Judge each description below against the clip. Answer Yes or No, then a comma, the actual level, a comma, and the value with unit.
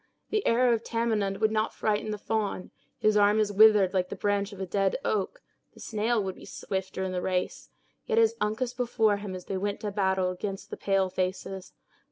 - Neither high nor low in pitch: No, high, 205 Hz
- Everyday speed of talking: No, fast, 210 wpm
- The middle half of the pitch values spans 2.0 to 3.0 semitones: Yes, narrow, 2.4 semitones